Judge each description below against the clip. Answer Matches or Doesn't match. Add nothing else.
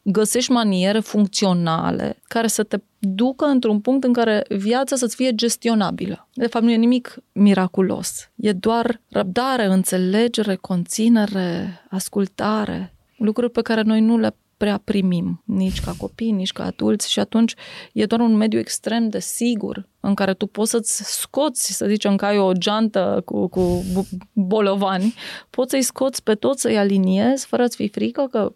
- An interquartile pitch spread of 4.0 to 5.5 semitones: Doesn't match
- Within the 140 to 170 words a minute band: Matches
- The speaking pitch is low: Doesn't match